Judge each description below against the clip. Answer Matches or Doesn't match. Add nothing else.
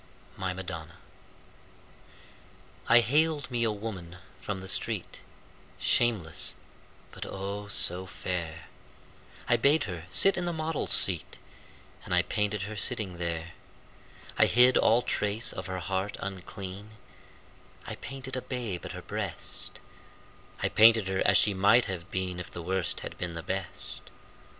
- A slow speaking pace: Doesn't match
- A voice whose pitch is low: Matches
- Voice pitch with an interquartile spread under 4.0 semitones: Doesn't match